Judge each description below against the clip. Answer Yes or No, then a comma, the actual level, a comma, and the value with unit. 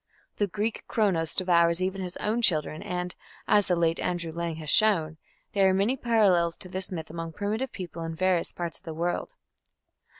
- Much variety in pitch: No, average, 3.3 semitones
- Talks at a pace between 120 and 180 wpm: No, average, 190 wpm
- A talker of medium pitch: Yes, medium, 180 Hz